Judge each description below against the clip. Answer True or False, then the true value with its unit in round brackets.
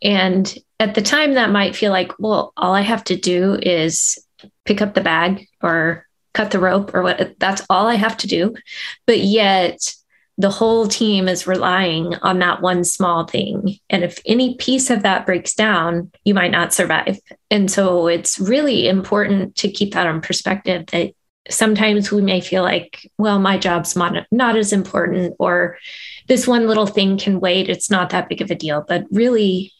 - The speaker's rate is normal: True (185 wpm)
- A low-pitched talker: False (195 Hz)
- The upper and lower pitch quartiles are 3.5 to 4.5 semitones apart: False (3.0 semitones)